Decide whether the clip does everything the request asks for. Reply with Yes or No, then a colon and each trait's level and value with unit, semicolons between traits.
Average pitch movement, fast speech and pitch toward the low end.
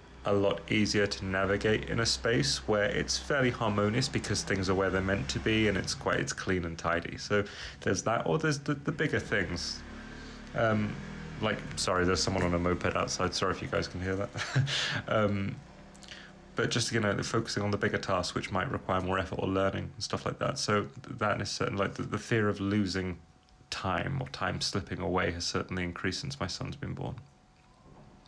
Yes: average, 3.7 semitones; fast, 205 wpm; low, 100 Hz